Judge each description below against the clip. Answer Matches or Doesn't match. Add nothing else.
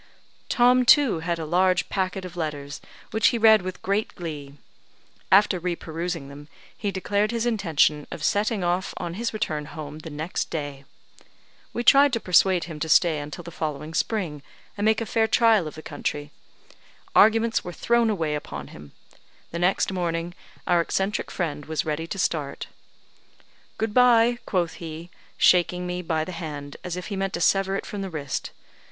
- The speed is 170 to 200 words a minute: Matches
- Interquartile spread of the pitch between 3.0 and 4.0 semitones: Doesn't match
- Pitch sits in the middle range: Matches